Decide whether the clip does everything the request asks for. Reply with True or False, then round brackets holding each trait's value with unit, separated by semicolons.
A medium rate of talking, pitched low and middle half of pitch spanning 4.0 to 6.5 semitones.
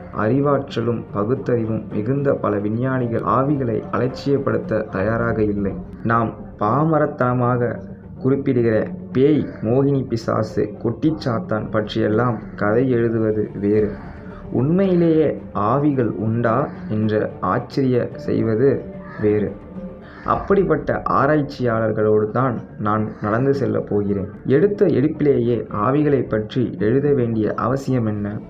True (90 wpm; 115 Hz; 4.4 semitones)